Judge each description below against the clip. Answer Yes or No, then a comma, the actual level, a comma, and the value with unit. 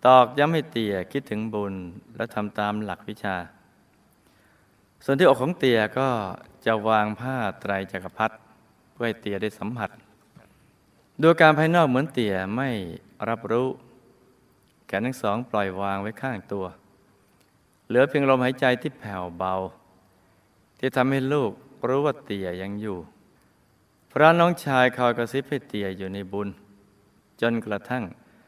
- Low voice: Yes, low, 110 Hz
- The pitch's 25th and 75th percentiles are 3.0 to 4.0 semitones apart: No, average, 4.6 semitones